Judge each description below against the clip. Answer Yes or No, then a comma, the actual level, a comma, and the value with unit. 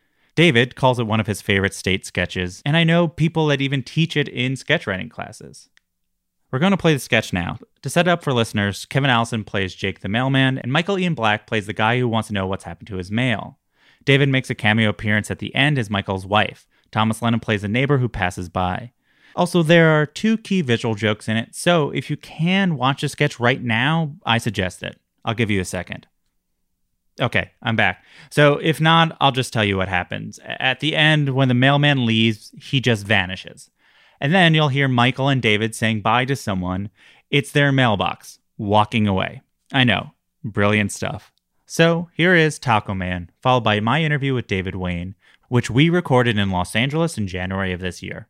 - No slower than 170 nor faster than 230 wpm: Yes, fast, 205 wpm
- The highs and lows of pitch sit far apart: Yes, wide, 6.0 semitones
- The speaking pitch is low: Yes, low, 120 Hz